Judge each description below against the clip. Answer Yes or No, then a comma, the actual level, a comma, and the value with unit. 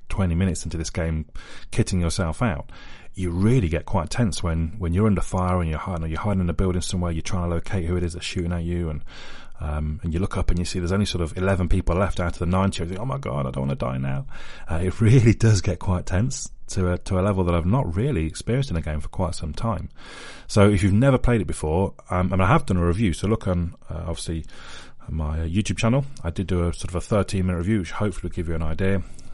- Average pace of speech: No, fast, 275 wpm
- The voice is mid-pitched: No, very low, 90 Hz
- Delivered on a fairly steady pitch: No, average, 3.0 semitones